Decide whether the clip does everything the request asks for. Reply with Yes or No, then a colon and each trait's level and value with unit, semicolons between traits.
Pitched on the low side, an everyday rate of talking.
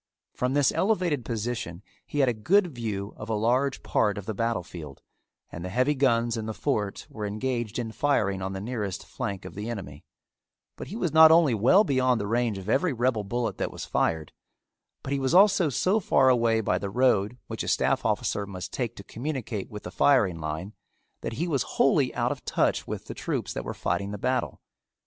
No: low, 115 Hz; fast, 210 wpm